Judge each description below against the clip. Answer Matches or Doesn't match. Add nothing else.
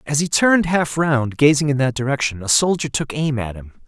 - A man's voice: Matches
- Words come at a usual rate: Doesn't match